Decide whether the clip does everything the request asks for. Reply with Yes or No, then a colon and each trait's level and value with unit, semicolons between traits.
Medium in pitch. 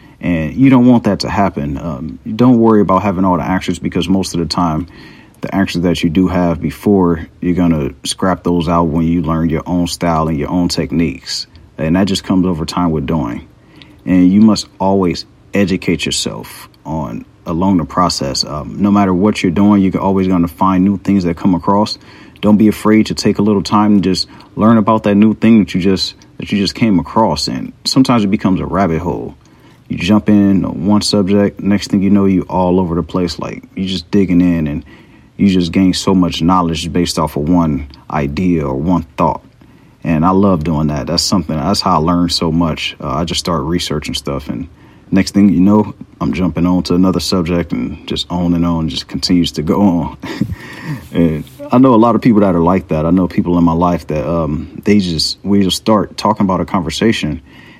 No: very low, 90 Hz